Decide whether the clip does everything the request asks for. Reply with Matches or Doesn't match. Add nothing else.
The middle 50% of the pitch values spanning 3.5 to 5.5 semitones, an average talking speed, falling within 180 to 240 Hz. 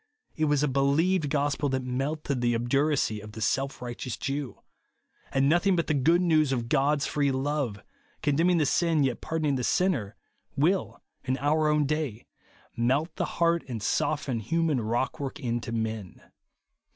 Doesn't match